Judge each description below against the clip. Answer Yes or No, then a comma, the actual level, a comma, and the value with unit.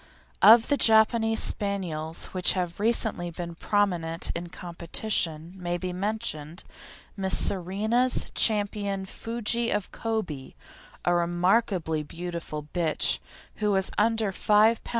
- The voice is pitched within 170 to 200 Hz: Yes, high, 190 Hz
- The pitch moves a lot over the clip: No, average, 4.2 semitones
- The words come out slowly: Yes, slow, 115 wpm